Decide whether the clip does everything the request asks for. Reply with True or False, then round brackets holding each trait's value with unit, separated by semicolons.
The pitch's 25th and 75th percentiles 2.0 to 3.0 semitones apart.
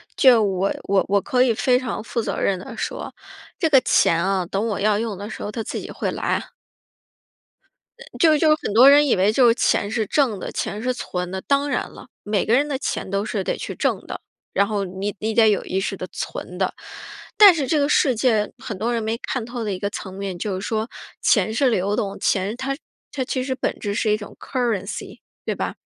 False (4.2 semitones)